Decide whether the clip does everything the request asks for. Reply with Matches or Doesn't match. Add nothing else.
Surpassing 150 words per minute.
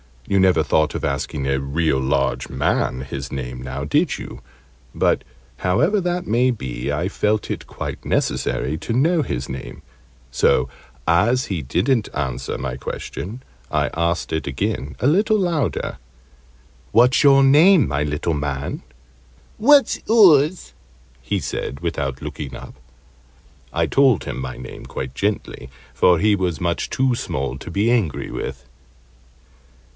Doesn't match